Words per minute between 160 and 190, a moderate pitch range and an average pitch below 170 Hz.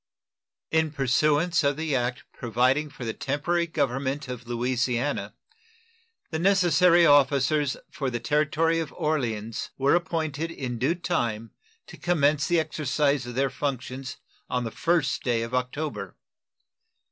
No: slow, 135 wpm; average, 3.9 semitones; medium, 140 Hz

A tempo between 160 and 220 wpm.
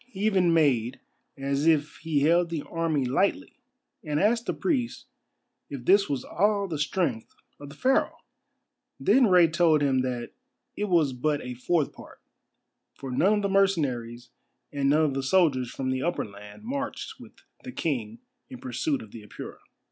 Yes: average, 170 wpm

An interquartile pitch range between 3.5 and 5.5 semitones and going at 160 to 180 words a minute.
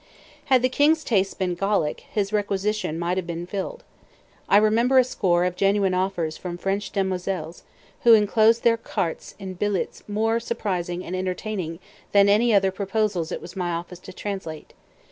No: average, 3.1 semitones; average, 165 wpm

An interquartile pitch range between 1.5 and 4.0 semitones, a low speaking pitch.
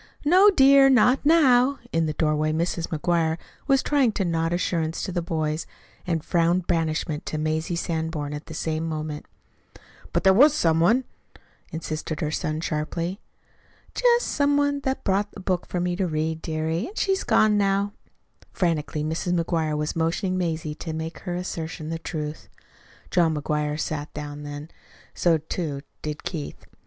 No: average, 3.7 semitones; medium, 165 Hz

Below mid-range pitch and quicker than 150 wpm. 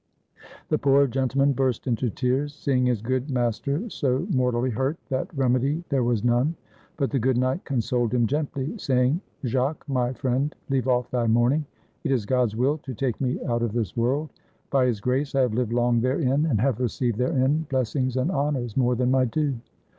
Yes: low, 130 Hz; average, 190 wpm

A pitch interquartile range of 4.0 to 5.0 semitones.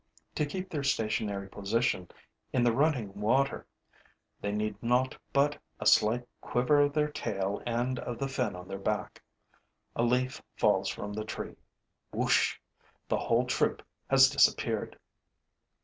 Yes: average, 4.3 semitones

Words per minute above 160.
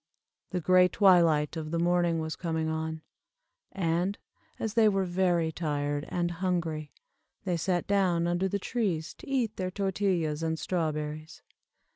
No: average, 145 wpm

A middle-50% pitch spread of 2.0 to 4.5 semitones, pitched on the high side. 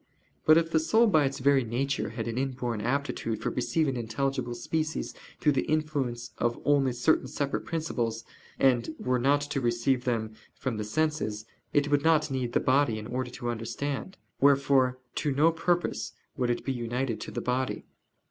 No: average, 3.3 semitones; low, 135 Hz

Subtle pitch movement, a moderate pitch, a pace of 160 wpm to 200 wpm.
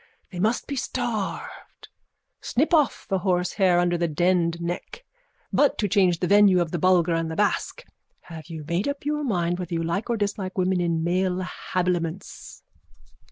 No: average, 3.2 semitones; medium, 180 Hz; average, 170 wpm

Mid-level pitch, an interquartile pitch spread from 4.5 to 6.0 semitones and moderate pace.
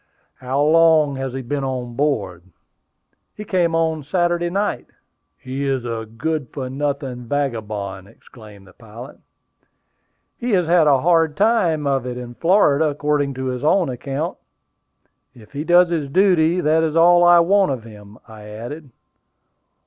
Yes: medium, 145 Hz; average, 5.1 semitones; average, 155 wpm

